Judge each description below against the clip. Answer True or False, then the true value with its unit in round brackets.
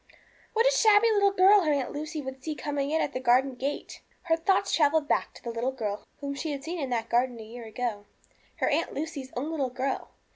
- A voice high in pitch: True (280 Hz)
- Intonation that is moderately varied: True (4.3 semitones)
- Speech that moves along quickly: True (230 wpm)